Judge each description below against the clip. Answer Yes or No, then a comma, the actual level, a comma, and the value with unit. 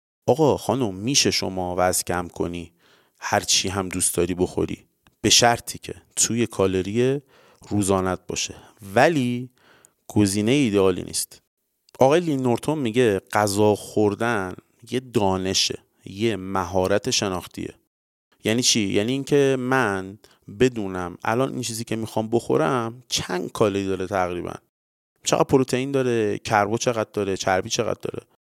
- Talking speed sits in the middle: No, slow, 125 wpm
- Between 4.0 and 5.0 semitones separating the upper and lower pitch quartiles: Yes, average, 4.5 semitones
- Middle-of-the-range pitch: No, low, 105 Hz